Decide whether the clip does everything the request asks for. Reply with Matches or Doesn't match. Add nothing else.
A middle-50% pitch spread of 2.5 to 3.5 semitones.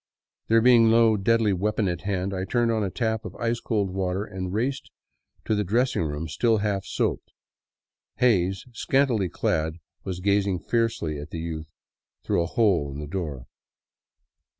Doesn't match